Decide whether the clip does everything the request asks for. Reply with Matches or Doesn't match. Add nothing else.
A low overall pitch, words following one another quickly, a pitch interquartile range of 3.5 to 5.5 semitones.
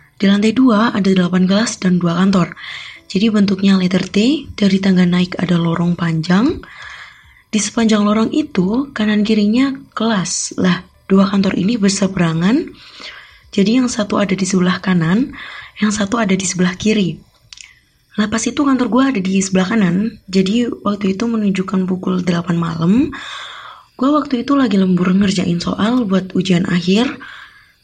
Doesn't match